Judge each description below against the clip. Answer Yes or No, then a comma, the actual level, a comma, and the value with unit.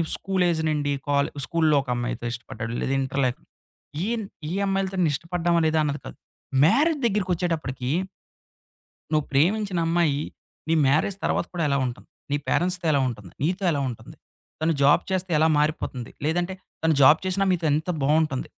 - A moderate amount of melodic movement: Yes, average, 4.2 semitones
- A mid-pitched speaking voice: Yes, medium, 160 Hz